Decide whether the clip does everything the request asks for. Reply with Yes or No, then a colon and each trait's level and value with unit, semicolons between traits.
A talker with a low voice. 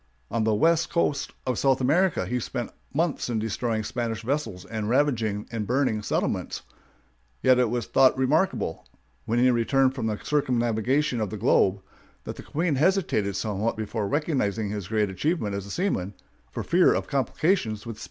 Yes: low, 120 Hz